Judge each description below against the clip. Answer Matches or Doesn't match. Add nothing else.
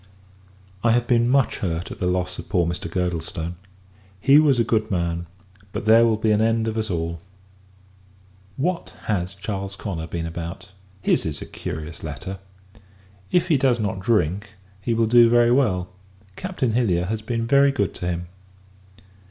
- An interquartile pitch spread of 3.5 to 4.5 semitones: Doesn't match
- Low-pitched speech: Matches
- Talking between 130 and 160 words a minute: Doesn't match